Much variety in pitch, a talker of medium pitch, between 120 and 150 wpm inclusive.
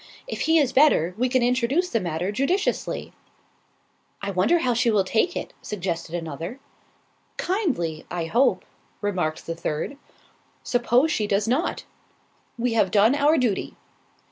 No: wide, 7.0 semitones; high, 230 Hz; average, 140 wpm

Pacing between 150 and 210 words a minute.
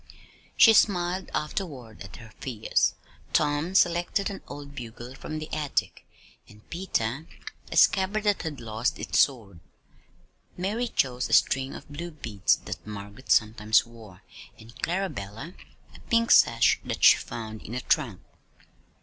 No: average, 140 wpm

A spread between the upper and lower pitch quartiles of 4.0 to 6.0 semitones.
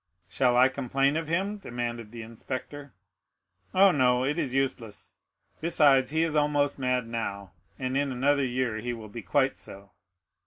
No: average, 3.4 semitones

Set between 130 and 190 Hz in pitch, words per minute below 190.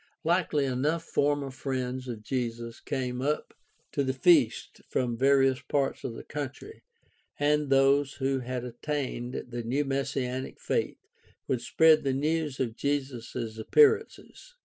Yes: low, 135 Hz; slow, 135 wpm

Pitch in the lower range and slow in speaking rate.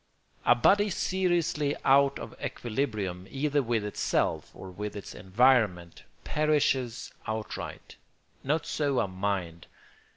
Yes: low, 120 Hz; slow, 110 wpm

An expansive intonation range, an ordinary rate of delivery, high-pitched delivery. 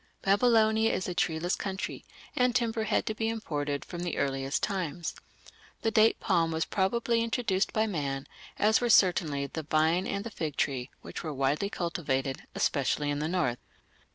No: wide, 6.8 semitones; average, 170 wpm; medium, 175 Hz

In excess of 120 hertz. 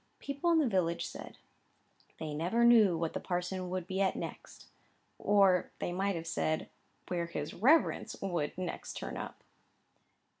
Yes: medium, 185 Hz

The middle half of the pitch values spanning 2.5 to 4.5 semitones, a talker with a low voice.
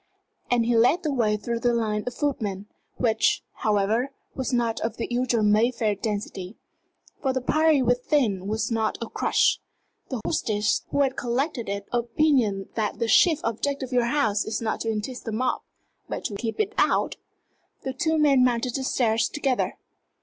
No: average, 3.3 semitones; high, 235 Hz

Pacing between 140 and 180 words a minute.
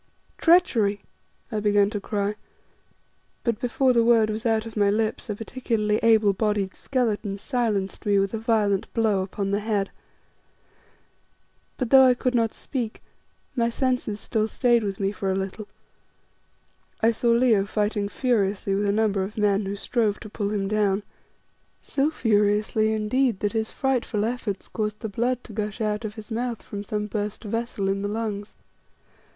Yes: average, 170 wpm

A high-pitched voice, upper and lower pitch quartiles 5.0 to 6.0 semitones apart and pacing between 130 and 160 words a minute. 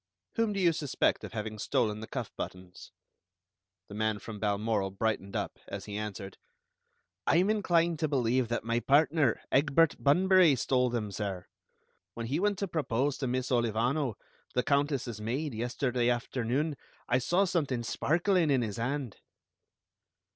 No: low, 125 Hz; wide, 5.6 semitones; average, 155 wpm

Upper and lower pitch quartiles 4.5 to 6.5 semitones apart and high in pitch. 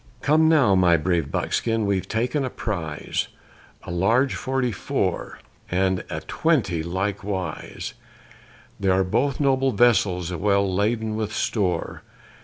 No: average, 5.0 semitones; low, 100 Hz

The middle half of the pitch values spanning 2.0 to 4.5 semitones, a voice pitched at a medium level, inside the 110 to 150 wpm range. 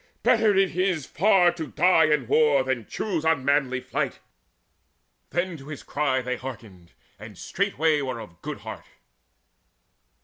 No: average, 5.1 semitones; medium, 150 Hz; average, 145 wpm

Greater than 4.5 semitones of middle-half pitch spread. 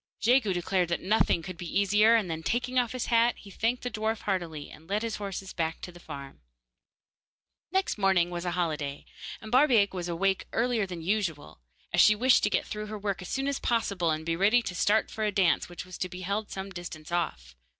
No: average, 4.1 semitones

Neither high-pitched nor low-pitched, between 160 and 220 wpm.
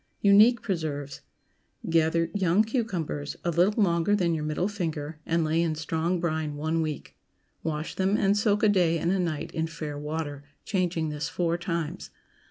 Yes: medium, 165 Hz; average, 175 wpm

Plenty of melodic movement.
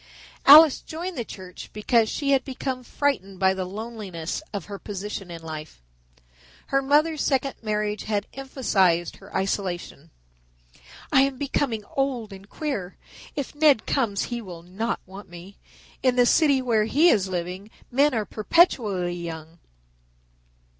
Yes: wide, 6.2 semitones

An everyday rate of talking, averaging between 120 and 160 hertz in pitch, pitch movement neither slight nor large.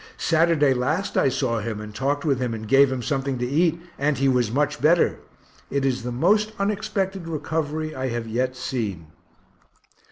Yes: average, 180 wpm; low, 135 Hz; average, 4.5 semitones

